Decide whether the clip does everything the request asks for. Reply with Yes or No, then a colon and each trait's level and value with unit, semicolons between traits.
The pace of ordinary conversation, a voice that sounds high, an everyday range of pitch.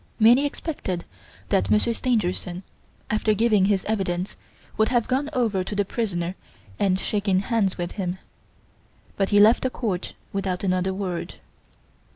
Yes: average, 145 wpm; high, 200 Hz; average, 3.3 semitones